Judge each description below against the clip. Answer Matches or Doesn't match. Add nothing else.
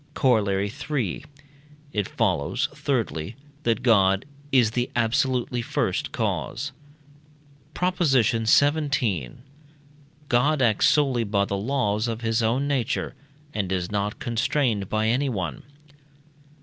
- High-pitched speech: Doesn't match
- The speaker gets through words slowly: Matches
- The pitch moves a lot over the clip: Doesn't match